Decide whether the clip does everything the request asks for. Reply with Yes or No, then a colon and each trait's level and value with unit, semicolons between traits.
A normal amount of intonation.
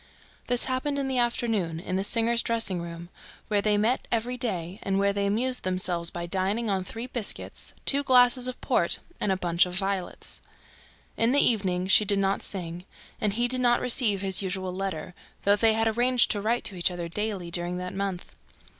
Yes: average, 4.5 semitones